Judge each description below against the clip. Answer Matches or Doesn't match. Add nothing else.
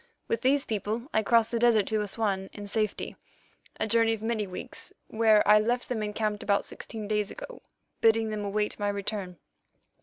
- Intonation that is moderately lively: Doesn't match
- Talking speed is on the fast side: Doesn't match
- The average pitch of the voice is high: Matches